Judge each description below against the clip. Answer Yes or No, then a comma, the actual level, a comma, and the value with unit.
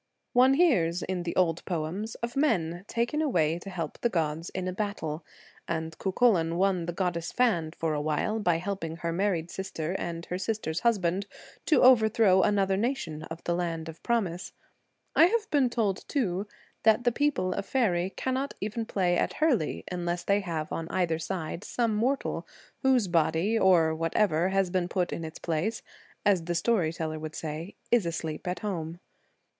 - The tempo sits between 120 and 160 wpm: No, average, 175 wpm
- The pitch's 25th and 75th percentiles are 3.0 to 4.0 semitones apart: No, average, 4.8 semitones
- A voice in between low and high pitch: Yes, medium, 180 Hz